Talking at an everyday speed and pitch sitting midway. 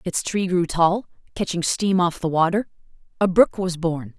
Yes: average, 185 wpm; medium, 180 Hz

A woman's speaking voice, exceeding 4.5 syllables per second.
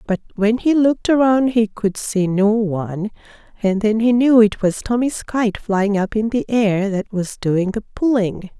No: female; 4.4 syllables/s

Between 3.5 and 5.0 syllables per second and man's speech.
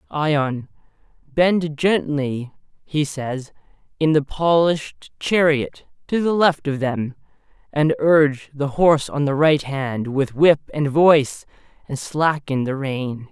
Yes: 3.6 syllables/s; male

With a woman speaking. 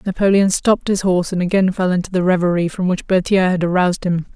Yes: female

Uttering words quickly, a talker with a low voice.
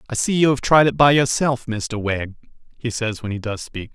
Yes: fast, 245 wpm; low, 120 Hz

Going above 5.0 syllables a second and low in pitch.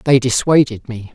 No: 4.9 syllables/s; low, 125 Hz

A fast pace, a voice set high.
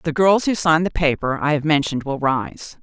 No: fast, 235 wpm; medium, 155 Hz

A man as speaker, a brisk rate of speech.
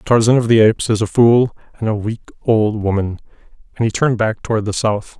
Yes: male; fast, 220 wpm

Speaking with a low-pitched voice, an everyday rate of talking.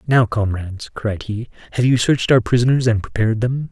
Yes: low, 115 Hz; average, 195 wpm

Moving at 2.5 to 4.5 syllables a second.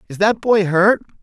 Yes: 4.4 syllables/s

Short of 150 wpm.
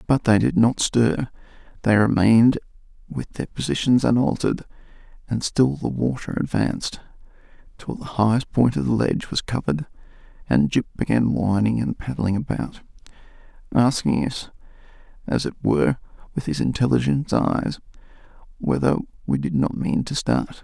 Yes: average, 140 wpm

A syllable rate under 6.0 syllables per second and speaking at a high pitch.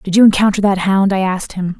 No: 6.3 syllables/s; high, 195 Hz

